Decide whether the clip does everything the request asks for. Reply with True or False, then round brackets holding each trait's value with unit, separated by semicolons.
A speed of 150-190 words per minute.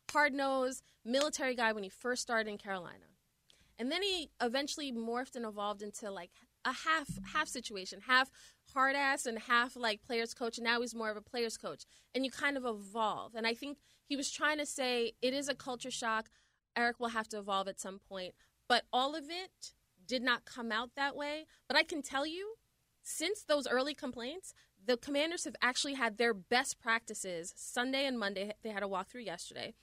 False (200 wpm)